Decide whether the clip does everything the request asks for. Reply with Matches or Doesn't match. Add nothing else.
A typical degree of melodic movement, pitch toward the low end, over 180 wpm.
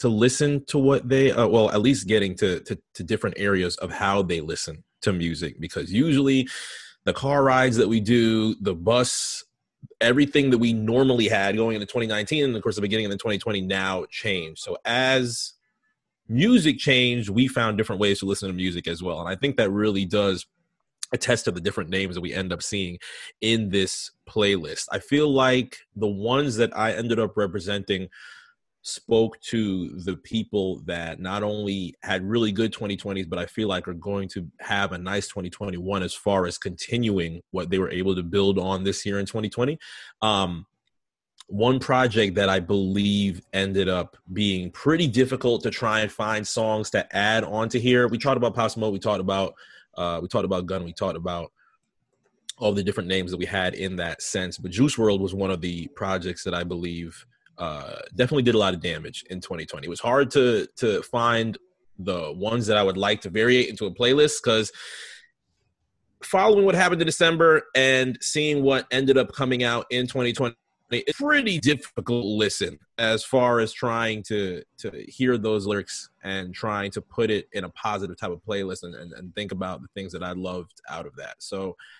Matches